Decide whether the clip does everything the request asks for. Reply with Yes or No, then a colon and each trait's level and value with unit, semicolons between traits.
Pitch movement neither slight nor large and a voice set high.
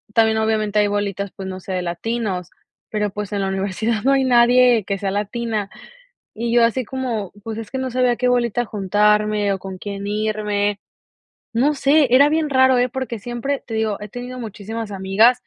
Yes: average, 3.2 semitones; high, 220 Hz